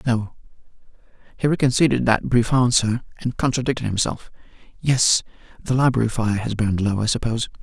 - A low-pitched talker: Yes, low, 115 Hz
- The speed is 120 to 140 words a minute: Yes, slow, 135 wpm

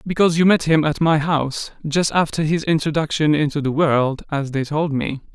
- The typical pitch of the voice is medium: Yes, medium, 155 Hz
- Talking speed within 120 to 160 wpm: No, average, 200 wpm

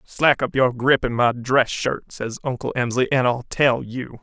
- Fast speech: Yes, fast, 215 wpm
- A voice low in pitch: Yes, low, 125 Hz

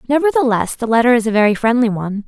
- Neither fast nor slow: No, fast, 210 wpm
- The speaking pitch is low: No, high, 235 Hz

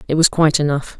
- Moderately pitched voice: Yes, medium, 150 Hz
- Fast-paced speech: Yes, fast, 240 wpm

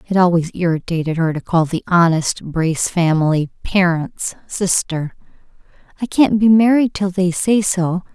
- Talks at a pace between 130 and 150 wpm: Yes, average, 145 wpm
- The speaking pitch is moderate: Yes, medium, 180 Hz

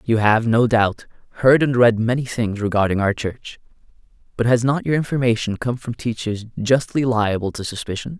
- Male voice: Yes, male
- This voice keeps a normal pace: Yes, average, 175 wpm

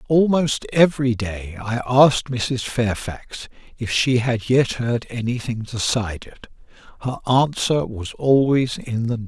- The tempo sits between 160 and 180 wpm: No, slow, 135 wpm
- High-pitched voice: No, low, 120 Hz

